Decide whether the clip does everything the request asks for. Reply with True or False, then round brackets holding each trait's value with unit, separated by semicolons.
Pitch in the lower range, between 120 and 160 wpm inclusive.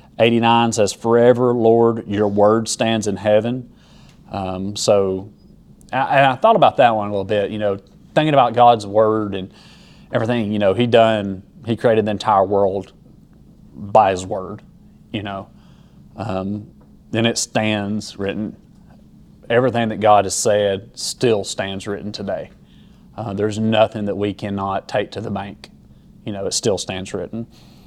True (105 Hz; 155 wpm)